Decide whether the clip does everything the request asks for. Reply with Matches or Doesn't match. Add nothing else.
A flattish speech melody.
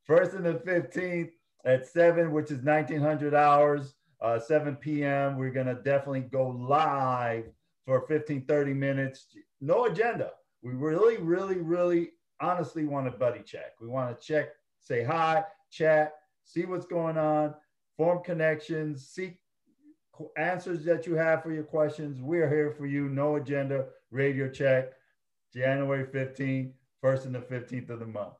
Doesn't match